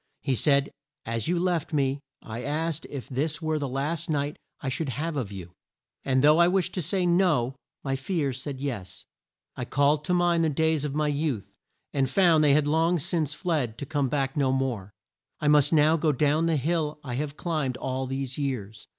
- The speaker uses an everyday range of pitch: Yes, average, 3.3 semitones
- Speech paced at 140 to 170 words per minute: No, average, 200 wpm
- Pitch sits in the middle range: Yes, medium, 145 Hz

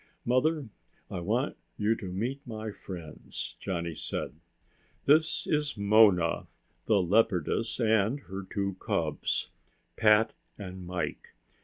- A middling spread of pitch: Yes, average, 4.0 semitones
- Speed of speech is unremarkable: No, slow, 115 wpm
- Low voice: Yes, low, 105 Hz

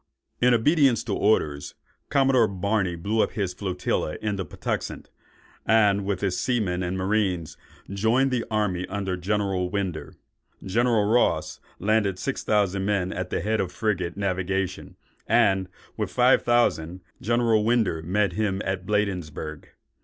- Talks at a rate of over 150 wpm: No, average, 140 wpm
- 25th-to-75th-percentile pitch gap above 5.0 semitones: No, average, 3.2 semitones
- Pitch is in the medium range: No, low, 100 Hz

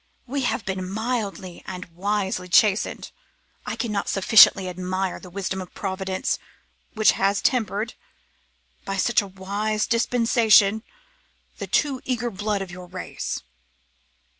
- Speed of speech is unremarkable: No, slow, 125 wpm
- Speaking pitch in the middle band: No, high, 200 Hz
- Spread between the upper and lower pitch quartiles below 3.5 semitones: Yes, average, 2.7 semitones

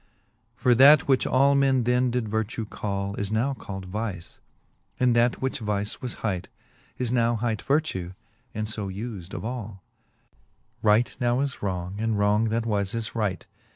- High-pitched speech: No, low, 110 Hz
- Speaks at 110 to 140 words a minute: No, average, 170 wpm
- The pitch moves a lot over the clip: No, average, 3.4 semitones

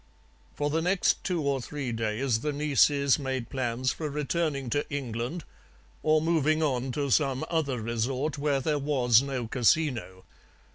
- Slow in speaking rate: No, average, 150 wpm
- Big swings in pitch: No, average, 3.3 semitones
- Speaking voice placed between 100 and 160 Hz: Yes, medium, 140 Hz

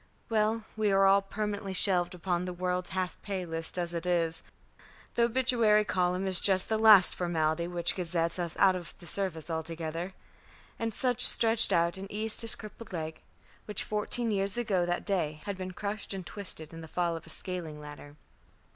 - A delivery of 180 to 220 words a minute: Yes, average, 185 wpm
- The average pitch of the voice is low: No, medium, 185 Hz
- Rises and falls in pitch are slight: No, average, 3.5 semitones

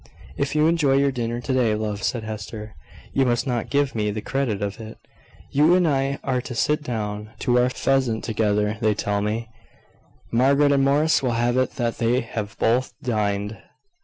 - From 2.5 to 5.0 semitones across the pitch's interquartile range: Yes, average, 4.0 semitones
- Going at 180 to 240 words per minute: Yes, average, 190 wpm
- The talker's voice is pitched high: No, low, 120 Hz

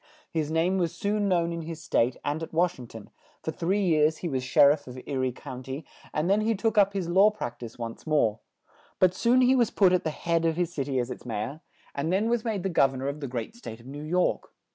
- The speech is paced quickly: Yes, fast, 275 wpm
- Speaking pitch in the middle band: Yes, medium, 160 Hz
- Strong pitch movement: Yes, wide, 6.1 semitones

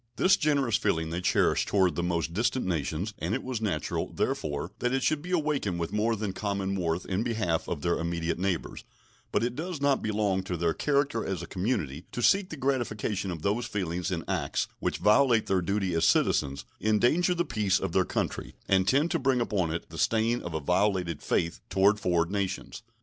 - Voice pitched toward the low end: Yes, low, 100 Hz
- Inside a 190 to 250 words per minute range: Yes, fast, 205 wpm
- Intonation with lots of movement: Yes, wide, 5.9 semitones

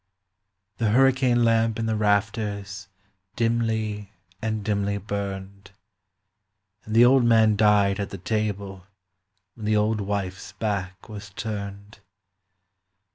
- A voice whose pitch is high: No, low, 105 Hz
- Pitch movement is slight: Yes, narrow, 1.9 semitones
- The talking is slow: Yes, slow, 115 wpm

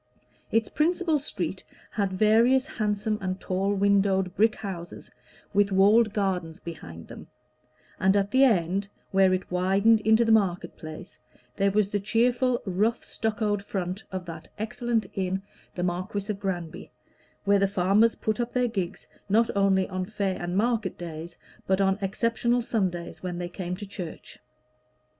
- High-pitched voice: Yes, high, 200 Hz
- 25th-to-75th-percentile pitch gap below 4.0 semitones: Yes, average, 2.9 semitones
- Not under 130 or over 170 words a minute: Yes, average, 155 wpm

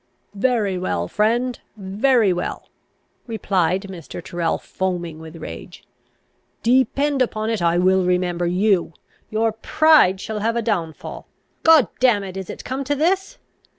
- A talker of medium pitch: No, high, 200 Hz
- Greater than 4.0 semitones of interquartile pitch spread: Yes, average, 5.1 semitones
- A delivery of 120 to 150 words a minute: Yes, average, 140 wpm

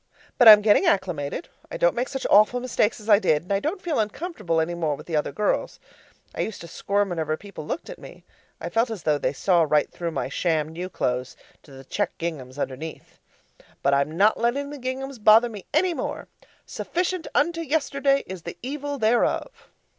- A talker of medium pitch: No, high, 205 Hz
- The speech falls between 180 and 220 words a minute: Yes, average, 200 wpm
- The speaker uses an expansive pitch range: Yes, wide, 8.8 semitones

